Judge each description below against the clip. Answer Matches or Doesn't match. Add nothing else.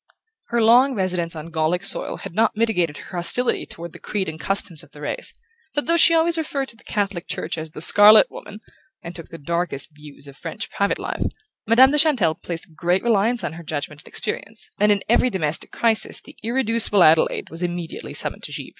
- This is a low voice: Doesn't match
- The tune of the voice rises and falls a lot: Matches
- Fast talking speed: Matches